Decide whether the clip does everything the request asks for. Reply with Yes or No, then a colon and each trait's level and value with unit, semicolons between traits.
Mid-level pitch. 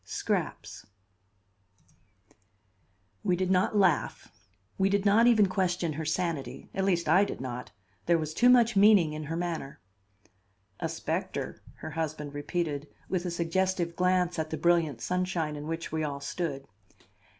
Yes: medium, 170 Hz